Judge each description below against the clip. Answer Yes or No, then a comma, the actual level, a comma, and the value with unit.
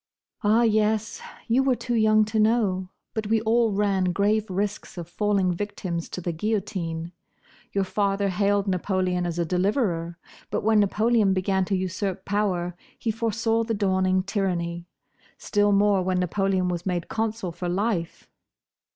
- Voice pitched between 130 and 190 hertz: No, high, 200 Hz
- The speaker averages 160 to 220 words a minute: No, average, 150 wpm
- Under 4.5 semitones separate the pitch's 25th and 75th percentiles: Yes, average, 2.9 semitones